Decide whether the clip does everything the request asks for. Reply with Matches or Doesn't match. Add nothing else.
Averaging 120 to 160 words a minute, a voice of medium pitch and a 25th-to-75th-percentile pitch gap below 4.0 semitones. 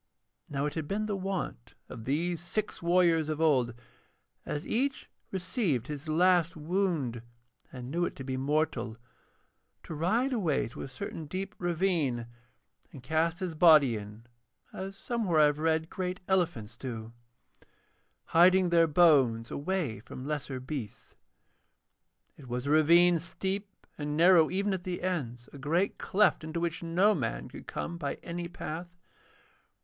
Doesn't match